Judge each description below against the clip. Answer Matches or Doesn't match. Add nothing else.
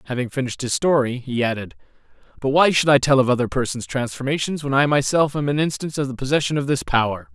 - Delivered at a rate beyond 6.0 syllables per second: Matches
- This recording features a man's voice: Matches